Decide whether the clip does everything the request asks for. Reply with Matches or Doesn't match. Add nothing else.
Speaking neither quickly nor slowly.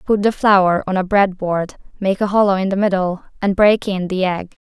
Doesn't match